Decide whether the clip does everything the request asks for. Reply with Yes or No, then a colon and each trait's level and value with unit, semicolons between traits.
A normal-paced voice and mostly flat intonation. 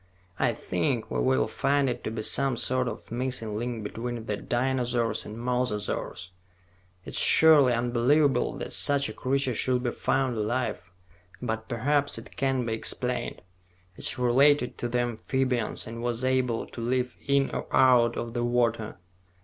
Yes: average, 165 wpm; narrow, 2.0 semitones